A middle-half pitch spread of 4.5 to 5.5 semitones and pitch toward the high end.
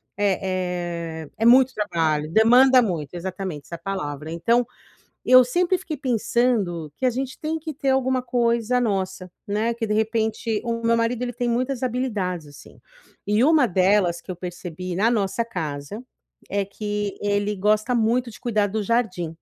Yes: average, 5.1 semitones; high, 215 Hz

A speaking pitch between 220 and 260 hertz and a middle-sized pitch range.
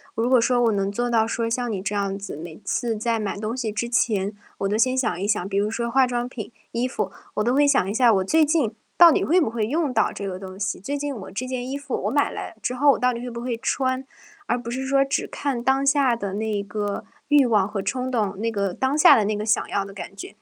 Yes: high, 235 Hz; average, 4.1 semitones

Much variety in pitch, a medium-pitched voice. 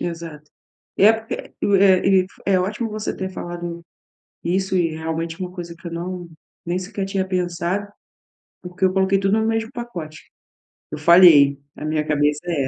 No: narrow, 2.6 semitones; medium, 180 Hz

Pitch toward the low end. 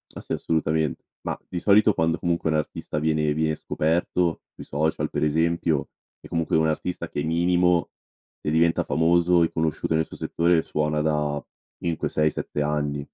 Yes: very low, 80 Hz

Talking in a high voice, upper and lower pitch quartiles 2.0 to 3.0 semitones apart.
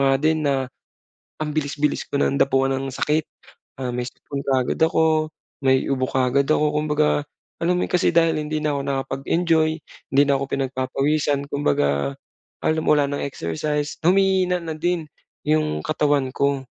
No: medium, 145 Hz; narrow, 2.6 semitones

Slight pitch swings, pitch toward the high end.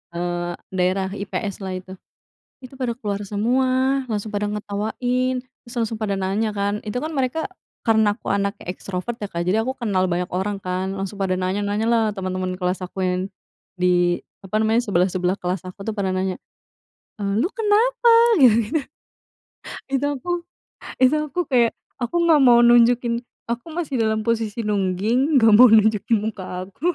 No: average, 4.2 semitones; high, 210 Hz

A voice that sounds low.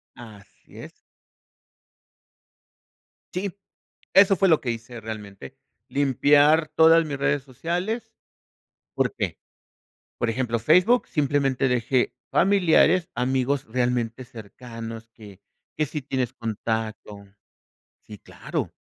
Yes: low, 130 Hz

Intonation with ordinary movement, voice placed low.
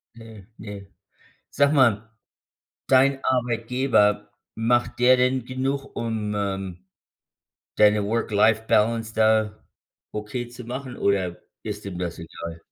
Yes: average, 3.2 semitones; low, 110 Hz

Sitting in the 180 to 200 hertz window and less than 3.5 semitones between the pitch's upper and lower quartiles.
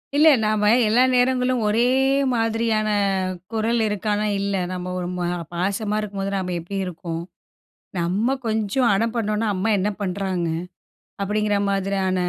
No: high, 210 Hz; average, 2.9 semitones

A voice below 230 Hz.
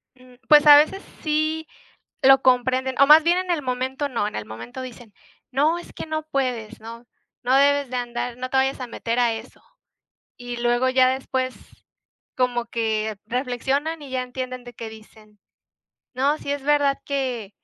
No: very high, 255 Hz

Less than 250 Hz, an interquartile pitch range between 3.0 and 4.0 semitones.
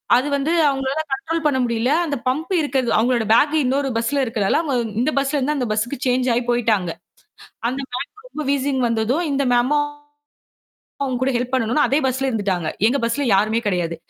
No: very high, 255 Hz; average, 3.4 semitones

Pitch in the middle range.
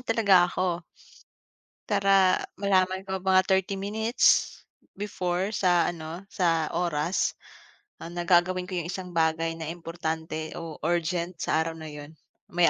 Yes: medium, 175 Hz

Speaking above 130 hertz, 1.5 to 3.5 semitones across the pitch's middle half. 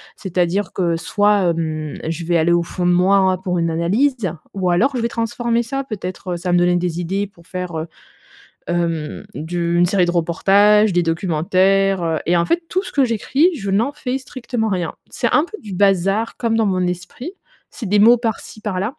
No: high, 190 Hz; average, 4.3 semitones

